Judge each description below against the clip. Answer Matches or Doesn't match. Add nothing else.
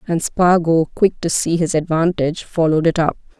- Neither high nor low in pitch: Matches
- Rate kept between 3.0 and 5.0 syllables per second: Doesn't match